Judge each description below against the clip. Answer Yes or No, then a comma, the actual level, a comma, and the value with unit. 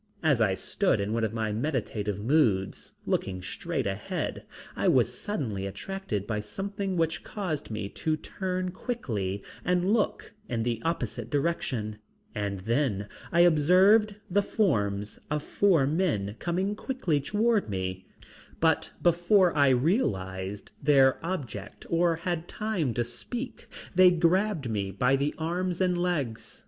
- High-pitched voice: No, medium, 150 Hz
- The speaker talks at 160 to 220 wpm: No, average, 140 wpm